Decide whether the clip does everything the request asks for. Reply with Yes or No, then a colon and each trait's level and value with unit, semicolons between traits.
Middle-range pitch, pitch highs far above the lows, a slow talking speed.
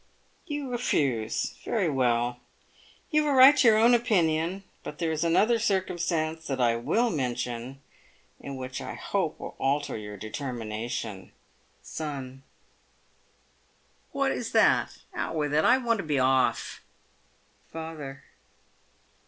Yes: medium, 150 Hz; wide, 7.5 semitones; slow, 130 wpm